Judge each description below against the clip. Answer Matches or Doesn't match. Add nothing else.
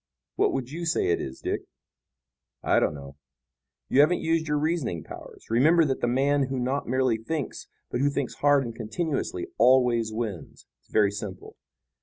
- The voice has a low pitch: Matches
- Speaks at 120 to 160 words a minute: Doesn't match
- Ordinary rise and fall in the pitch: Matches